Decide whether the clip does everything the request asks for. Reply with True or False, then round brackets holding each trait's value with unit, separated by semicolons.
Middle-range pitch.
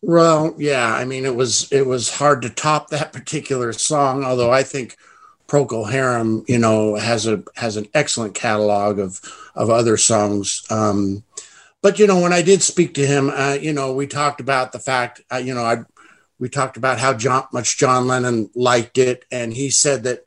False (130 Hz)